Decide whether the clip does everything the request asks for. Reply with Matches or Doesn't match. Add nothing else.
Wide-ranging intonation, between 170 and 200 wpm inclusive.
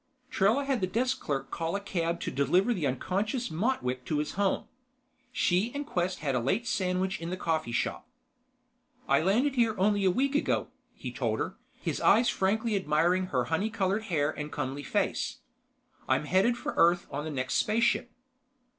Matches